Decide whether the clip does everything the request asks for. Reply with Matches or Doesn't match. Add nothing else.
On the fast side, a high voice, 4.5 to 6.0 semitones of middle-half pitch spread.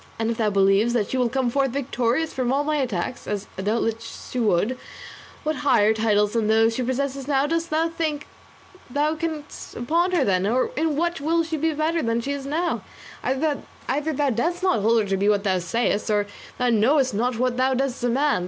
Matches